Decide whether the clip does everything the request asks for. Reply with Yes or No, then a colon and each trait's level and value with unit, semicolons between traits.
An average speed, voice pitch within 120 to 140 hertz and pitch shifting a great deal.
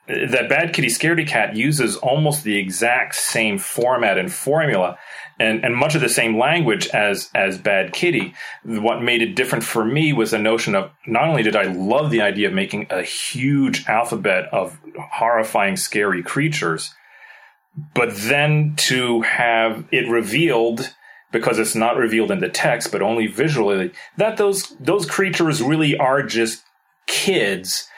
Yes: average, 160 wpm; low, 135 Hz; wide, 5.7 semitones